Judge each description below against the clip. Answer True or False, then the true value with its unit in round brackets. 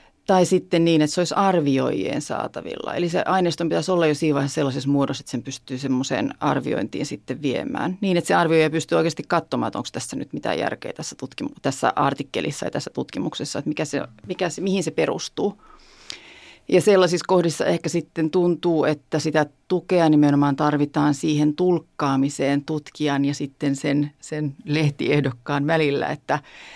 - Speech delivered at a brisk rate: True (165 wpm)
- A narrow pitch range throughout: False (3.2 semitones)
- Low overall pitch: False (155 Hz)